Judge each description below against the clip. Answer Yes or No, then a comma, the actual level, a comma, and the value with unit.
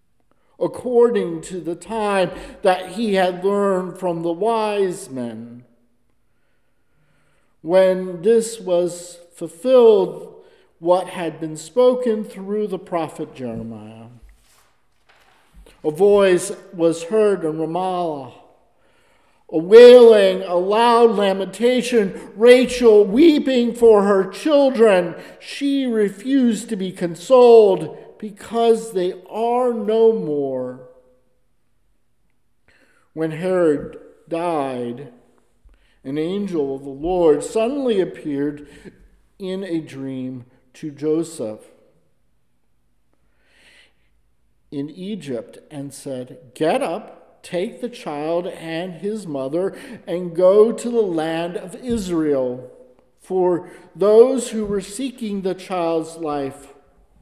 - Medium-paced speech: No, slow, 95 wpm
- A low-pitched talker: No, medium, 180 Hz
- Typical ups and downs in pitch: No, wide, 6.2 semitones